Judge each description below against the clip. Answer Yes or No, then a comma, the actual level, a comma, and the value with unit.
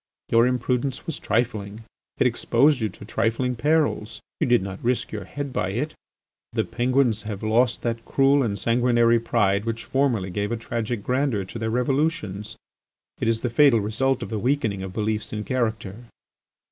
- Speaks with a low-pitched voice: Yes, low, 115 Hz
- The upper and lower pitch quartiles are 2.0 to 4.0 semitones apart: Yes, average, 3.0 semitones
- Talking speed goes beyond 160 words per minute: Yes, average, 170 wpm